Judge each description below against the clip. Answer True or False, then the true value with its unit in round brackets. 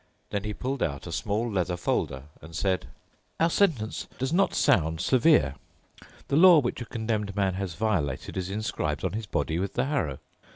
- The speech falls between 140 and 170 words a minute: False (180 wpm)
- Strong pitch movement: True (5.9 semitones)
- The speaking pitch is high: False (105 Hz)